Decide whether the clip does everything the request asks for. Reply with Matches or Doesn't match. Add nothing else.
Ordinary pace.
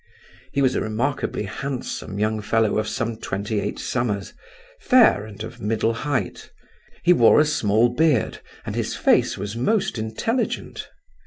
Matches